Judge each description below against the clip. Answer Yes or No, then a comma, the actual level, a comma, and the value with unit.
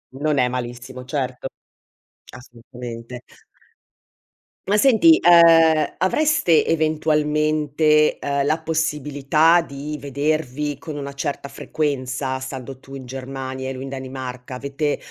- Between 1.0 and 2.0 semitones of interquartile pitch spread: No, average, 2.9 semitones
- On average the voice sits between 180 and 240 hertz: No, medium, 140 Hz